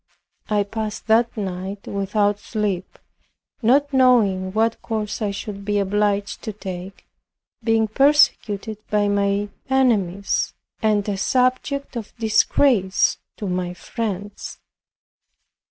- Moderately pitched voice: No, high, 210 Hz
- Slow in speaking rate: Yes, slow, 110 wpm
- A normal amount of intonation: No, narrow, 2.2 semitones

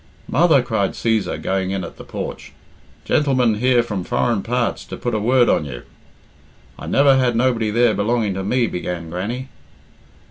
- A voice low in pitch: Yes, low, 115 Hz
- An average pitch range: Yes, average, 4.2 semitones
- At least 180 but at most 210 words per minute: No, average, 170 wpm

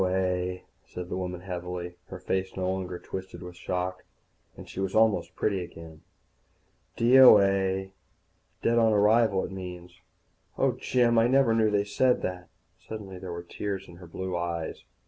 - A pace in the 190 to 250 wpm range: No, average, 165 wpm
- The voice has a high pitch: No, very low, 95 Hz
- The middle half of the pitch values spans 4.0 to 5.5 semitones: No, narrow, 2.4 semitones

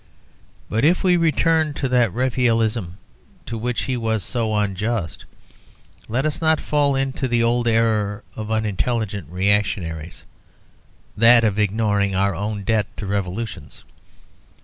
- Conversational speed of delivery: No, slow, 130 wpm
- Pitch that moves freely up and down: No, average, 3.3 semitones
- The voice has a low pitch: Yes, low, 110 Hz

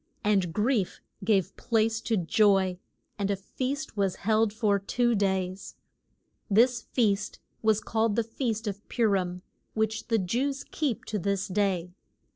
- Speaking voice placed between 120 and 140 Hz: No, high, 210 Hz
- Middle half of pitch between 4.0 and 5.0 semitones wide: No, average, 2.7 semitones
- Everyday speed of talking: Yes, average, 145 wpm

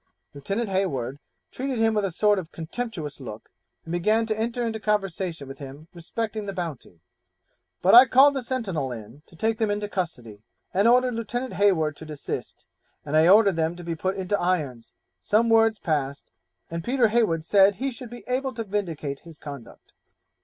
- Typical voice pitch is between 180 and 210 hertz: Yes, high, 190 Hz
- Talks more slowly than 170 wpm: No, average, 180 wpm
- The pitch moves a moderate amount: No, wide, 6.1 semitones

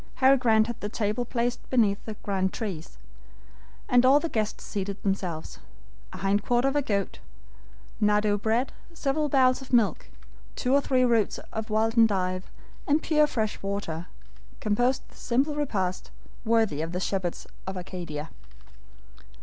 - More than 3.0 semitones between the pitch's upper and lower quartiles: Yes, average, 4.5 semitones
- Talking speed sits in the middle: Yes, average, 150 wpm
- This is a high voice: Yes, high, 220 Hz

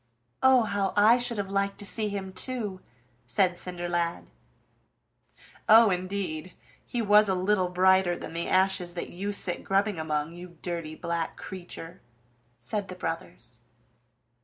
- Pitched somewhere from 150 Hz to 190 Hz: Yes, medium, 185 Hz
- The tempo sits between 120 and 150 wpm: Yes, average, 140 wpm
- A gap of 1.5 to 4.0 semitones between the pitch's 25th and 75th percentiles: Yes, average, 2.8 semitones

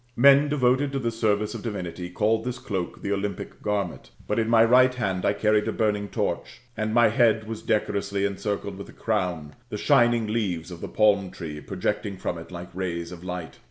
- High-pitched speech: No, low, 105 Hz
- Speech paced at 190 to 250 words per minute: Yes, average, 200 wpm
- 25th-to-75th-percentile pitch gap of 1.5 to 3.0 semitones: No, average, 3.8 semitones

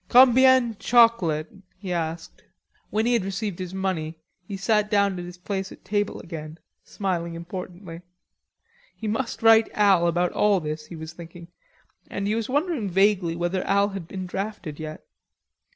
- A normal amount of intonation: Yes, average, 3.8 semitones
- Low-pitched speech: No, high, 190 Hz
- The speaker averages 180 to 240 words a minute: No, average, 160 wpm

